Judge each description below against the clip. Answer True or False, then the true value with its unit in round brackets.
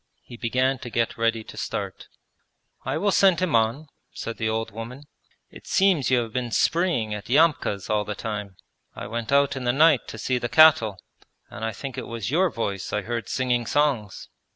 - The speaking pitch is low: True (120 Hz)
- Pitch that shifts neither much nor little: True (4.1 semitones)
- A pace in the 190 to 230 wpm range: True (200 wpm)